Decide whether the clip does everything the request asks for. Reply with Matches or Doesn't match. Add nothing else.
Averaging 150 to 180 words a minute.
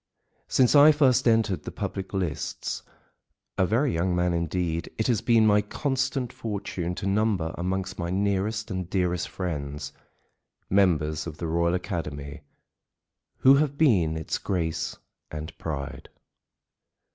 Doesn't match